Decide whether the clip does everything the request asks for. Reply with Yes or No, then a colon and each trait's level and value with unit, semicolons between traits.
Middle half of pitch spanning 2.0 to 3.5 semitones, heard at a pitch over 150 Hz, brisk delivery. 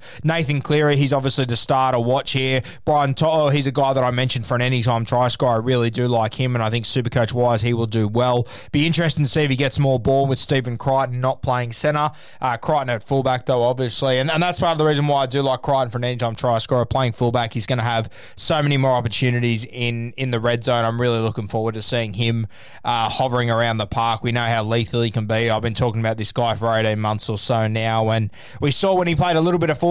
No: average, 2.8 semitones; low, 125 Hz; fast, 265 wpm